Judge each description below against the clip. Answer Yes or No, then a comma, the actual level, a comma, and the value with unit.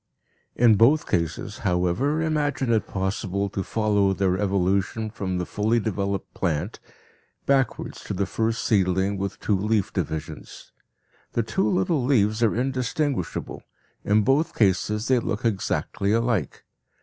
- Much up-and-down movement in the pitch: No, average, 3.7 semitones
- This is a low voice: Yes, low, 105 Hz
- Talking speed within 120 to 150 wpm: Yes, slow, 135 wpm